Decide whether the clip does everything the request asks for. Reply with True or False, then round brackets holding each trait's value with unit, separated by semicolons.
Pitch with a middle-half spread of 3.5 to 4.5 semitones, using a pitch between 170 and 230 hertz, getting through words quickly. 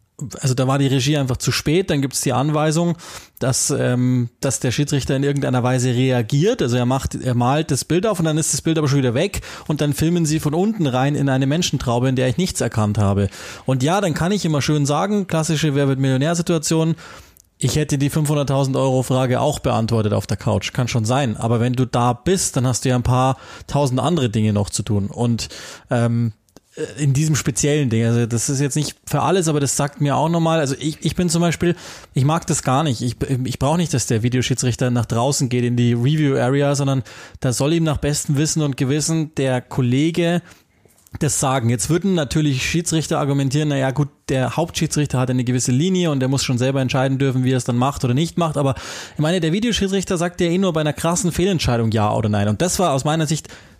False (3.8 semitones; 140 Hz; 225 wpm)